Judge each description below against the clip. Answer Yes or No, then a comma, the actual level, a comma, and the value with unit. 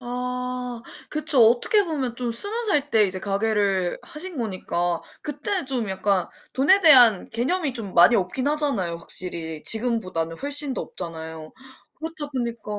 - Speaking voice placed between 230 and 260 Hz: Yes, high, 240 Hz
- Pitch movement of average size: No, wide, 7.3 semitones